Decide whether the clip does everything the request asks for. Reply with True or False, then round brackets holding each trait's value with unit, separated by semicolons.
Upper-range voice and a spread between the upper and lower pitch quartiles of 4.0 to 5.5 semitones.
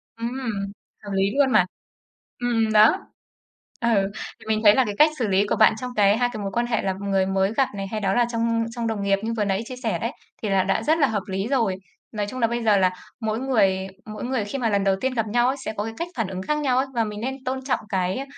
False (220 Hz; 3.5 semitones)